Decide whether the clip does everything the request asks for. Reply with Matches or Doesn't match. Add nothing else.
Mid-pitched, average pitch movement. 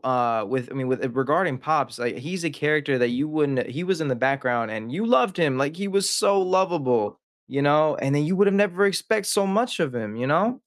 Doesn't match